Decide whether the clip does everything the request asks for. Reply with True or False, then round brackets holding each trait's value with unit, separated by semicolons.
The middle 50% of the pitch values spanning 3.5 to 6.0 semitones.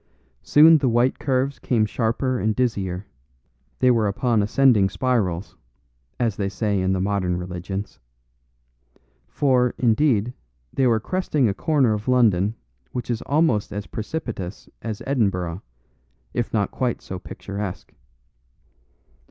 True (4.4 semitones)